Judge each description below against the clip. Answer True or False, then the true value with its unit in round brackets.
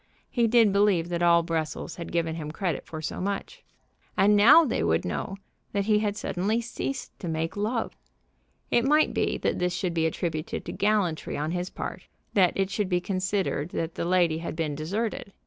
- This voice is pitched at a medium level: True (180 Hz)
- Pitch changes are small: False (4.1 semitones)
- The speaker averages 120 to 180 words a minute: False (195 wpm)